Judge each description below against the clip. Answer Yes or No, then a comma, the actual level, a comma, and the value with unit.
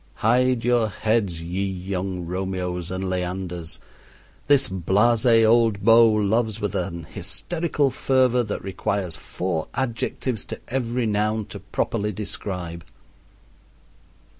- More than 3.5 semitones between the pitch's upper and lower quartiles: Yes, average, 4.2 semitones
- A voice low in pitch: Yes, low, 105 Hz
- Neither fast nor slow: No, slow, 115 wpm